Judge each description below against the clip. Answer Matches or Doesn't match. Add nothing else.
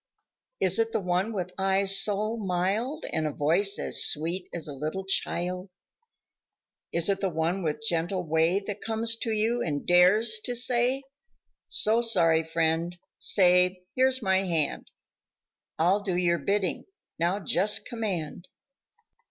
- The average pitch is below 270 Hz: Matches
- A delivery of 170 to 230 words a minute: Doesn't match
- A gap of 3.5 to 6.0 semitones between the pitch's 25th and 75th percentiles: Matches